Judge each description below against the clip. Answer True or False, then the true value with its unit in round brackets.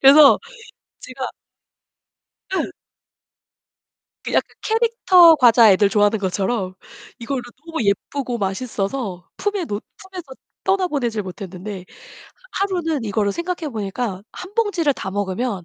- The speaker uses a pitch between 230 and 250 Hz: True (245 Hz)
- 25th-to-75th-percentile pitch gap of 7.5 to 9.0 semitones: True (8.7 semitones)